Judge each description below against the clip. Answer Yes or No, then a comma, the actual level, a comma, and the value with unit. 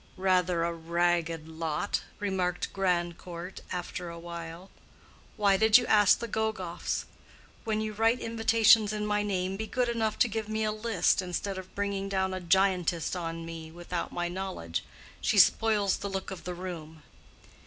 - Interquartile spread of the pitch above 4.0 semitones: No, average, 3.4 semitones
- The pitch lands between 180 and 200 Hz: Yes, high, 190 Hz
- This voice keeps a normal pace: Yes, average, 165 wpm